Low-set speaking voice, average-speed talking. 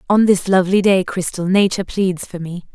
No: medium, 185 Hz; average, 195 wpm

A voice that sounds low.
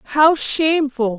No: very high, 285 Hz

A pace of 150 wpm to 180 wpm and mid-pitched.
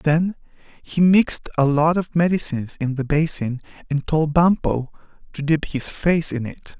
Yes: average, 170 wpm; medium, 155 Hz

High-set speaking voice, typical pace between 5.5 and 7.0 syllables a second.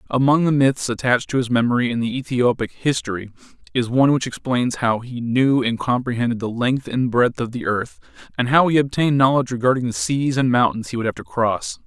No: low, 125 Hz; 5.9 syllables/s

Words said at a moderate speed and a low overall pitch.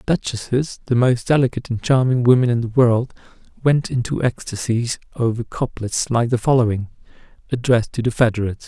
Yes: average, 150 wpm; low, 120 Hz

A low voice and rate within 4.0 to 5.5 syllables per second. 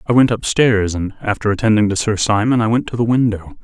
No: low, 110 Hz; 6.0 syllables/s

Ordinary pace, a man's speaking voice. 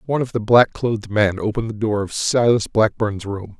No: fast, 215 wpm; male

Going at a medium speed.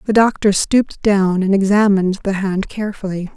Yes: average, 160 wpm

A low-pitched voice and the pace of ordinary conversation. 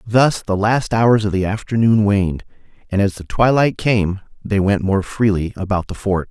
Yes: low, 105 Hz; average, 190 wpm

